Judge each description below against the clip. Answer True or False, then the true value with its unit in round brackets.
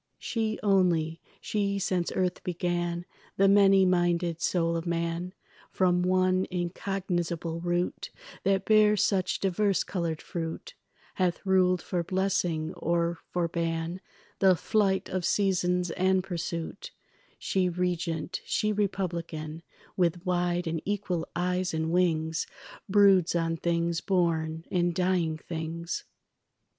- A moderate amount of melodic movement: False (2.0 semitones)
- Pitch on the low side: False (175 Hz)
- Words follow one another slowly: True (120 wpm)